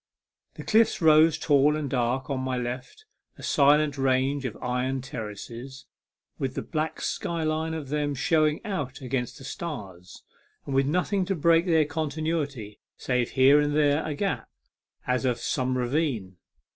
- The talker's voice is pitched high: No, medium, 140 Hz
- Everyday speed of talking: Yes, average, 160 wpm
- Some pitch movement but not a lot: Yes, average, 3.4 semitones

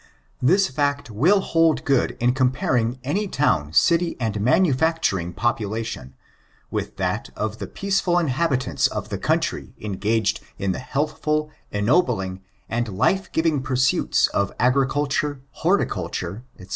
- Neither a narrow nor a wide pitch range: No, wide, 6.5 semitones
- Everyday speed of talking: No, slow, 130 wpm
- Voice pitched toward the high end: No, low, 130 Hz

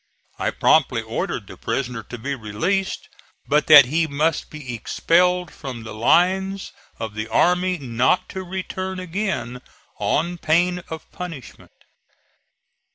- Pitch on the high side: No, medium, 160 Hz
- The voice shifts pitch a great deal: Yes, wide, 6.5 semitones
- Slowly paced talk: Yes, slow, 130 wpm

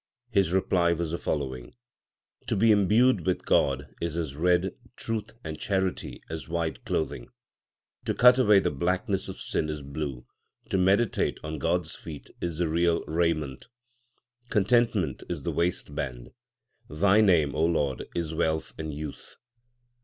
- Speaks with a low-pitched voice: Yes, very low, 85 Hz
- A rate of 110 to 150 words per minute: Yes, average, 145 wpm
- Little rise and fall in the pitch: No, average, 3.7 semitones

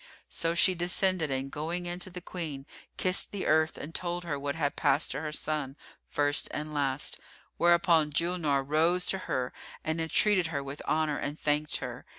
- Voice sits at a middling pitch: Yes, medium, 155 Hz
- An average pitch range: Yes, average, 3.1 semitones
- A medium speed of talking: Yes, average, 180 wpm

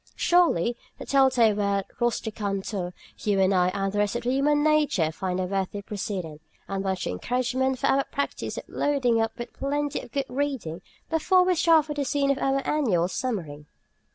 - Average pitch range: No, wide, 6.3 semitones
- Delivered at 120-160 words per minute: No, average, 180 wpm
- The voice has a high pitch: Yes, high, 235 Hz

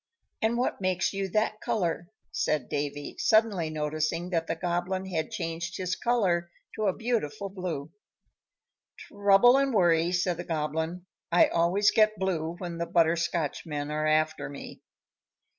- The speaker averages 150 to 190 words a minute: No, average, 140 wpm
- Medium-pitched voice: Yes, medium, 175 Hz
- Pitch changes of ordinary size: Yes, average, 3.5 semitones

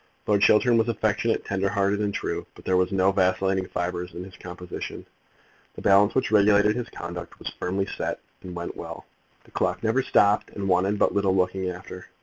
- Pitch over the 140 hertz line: No, very low, 95 Hz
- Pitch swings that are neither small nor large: No, narrow, 2.1 semitones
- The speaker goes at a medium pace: Yes, average, 190 wpm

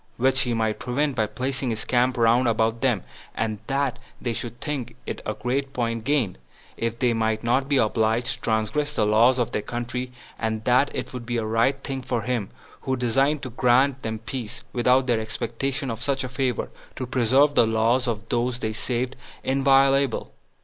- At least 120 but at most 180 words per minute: No, average, 190 wpm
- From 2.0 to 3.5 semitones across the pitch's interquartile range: Yes, average, 2.8 semitones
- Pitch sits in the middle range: No, low, 125 Hz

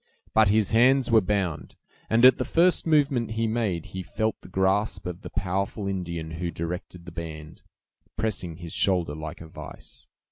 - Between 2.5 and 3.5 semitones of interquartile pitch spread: No, average, 4.6 semitones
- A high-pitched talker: No, very low, 95 Hz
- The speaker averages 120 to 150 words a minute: No, average, 175 wpm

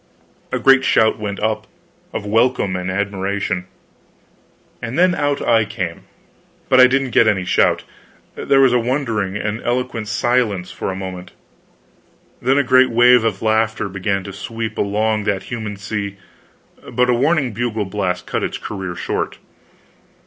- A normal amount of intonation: Yes, average, 3.8 semitones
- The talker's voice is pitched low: Yes, low, 110 Hz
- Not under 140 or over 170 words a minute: Yes, average, 155 wpm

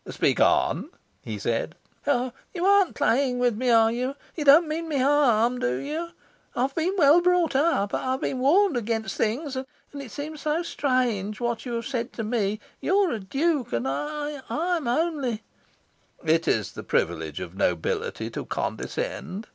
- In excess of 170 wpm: Yes, average, 185 wpm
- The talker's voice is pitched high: Yes, very high, 260 Hz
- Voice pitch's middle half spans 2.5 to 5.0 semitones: No, wide, 5.5 semitones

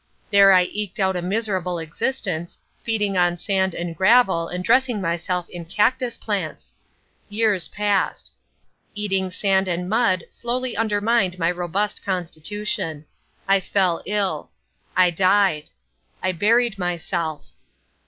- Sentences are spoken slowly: Yes, slow, 125 wpm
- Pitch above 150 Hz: Yes, high, 190 Hz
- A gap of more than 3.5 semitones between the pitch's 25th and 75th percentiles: No, average, 3.0 semitones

